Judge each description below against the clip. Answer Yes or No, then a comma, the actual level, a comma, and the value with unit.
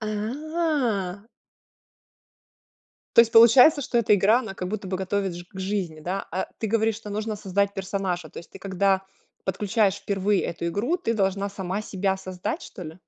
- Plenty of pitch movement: No, average, 2.7 semitones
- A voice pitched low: No, high, 200 Hz